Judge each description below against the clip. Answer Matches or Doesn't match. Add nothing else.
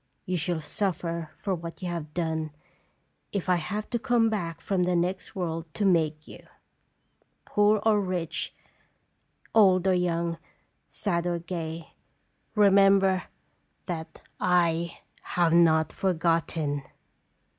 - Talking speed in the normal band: Doesn't match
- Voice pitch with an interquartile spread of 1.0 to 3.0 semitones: Matches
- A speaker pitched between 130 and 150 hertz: Doesn't match